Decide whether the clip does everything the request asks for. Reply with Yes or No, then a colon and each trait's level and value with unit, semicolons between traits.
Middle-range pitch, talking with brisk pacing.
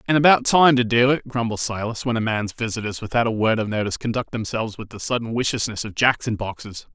No: low, 115 Hz; fast, 235 wpm